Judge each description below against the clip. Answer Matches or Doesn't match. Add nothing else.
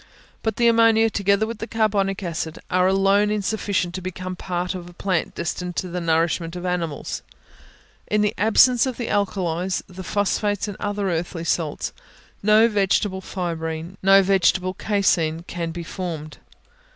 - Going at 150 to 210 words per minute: Matches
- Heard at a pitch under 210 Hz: Matches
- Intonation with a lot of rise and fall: Doesn't match